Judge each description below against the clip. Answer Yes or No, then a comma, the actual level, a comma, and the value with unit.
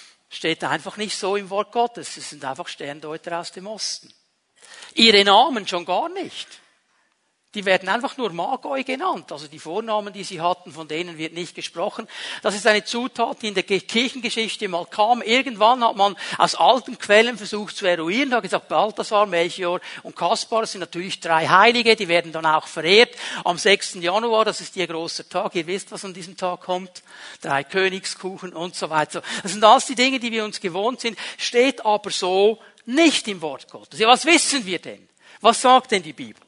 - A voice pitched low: No, high, 200 Hz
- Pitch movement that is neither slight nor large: Yes, average, 4.7 semitones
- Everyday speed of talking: No, fast, 195 wpm